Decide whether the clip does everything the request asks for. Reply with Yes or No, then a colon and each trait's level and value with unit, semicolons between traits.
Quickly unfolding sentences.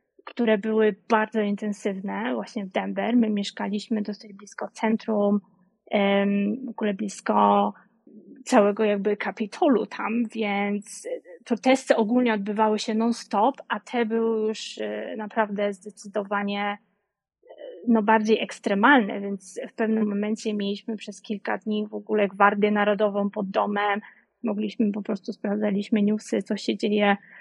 No: average, 125 wpm